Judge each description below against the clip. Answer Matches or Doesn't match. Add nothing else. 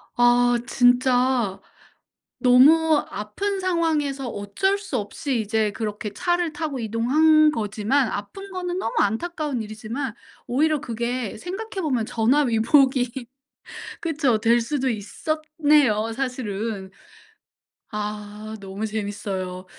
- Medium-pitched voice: Doesn't match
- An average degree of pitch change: Doesn't match